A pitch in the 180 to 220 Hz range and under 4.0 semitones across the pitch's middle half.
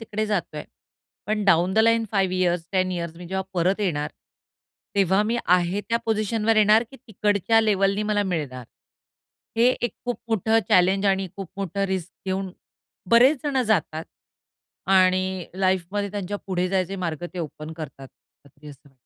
Yes: high, 190 Hz; average, 3.2 semitones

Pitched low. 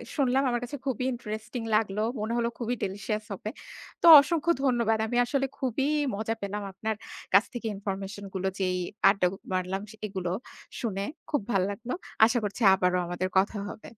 No: high, 215 Hz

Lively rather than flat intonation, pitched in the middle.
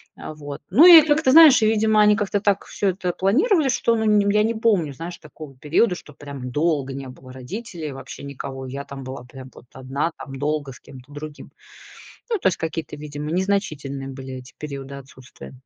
Yes: wide, 7.2 semitones; medium, 150 Hz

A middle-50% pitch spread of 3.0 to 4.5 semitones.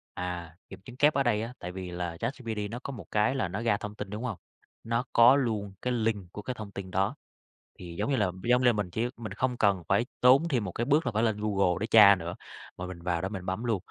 Yes: average, 4.2 semitones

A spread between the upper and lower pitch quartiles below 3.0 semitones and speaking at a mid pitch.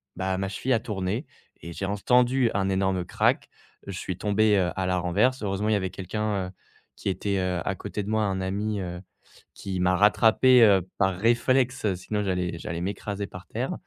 No: narrow, 2.6 semitones; low, 100 Hz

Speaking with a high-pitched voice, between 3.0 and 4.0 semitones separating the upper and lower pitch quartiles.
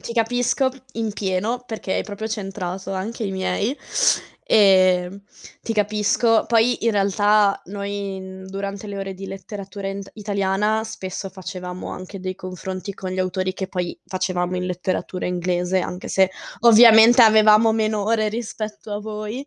No: high, 200 Hz; narrow, 2.5 semitones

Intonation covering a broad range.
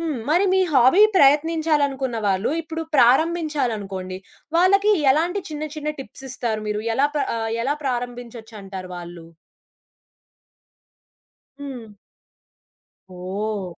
Yes: wide, 6.6 semitones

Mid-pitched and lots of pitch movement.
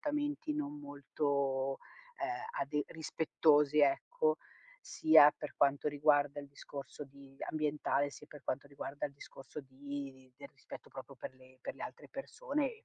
Yes: medium, 145 Hz; wide, 5.8 semitones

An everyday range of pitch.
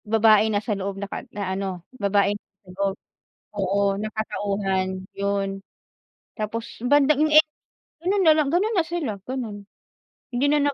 No: wide, 6.1 semitones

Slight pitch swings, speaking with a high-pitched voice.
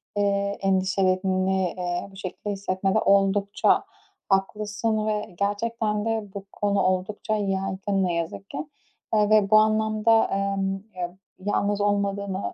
Yes: narrow, 1.6 semitones; high, 200 Hz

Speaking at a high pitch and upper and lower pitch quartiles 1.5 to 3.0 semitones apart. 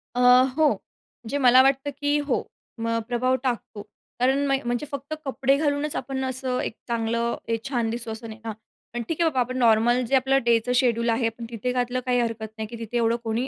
Yes: high, 245 Hz; narrow, 2.5 semitones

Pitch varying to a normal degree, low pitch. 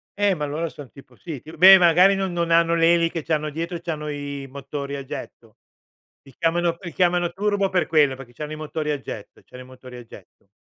No: average, 3.5 semitones; medium, 160 Hz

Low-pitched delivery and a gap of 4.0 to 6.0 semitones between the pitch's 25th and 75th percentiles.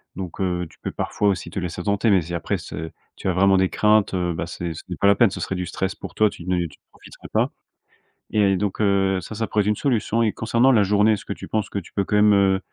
No: very low, 95 Hz; average, 2.7 semitones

